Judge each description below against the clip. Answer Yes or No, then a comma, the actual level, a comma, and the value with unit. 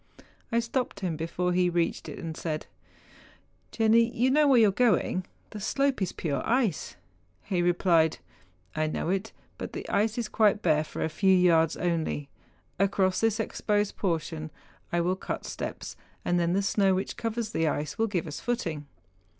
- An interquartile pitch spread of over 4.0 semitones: Yes, average, 5.2 semitones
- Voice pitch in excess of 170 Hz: Yes, medium, 185 Hz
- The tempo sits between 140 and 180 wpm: No, average, 190 wpm